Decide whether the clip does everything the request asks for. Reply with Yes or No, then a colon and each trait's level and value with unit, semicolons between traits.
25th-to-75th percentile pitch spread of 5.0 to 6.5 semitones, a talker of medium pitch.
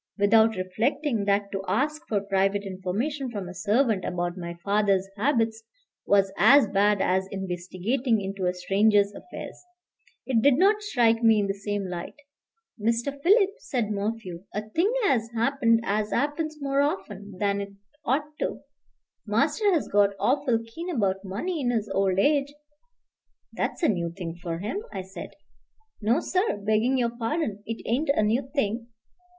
No: wide, 5.4 semitones; high, 215 Hz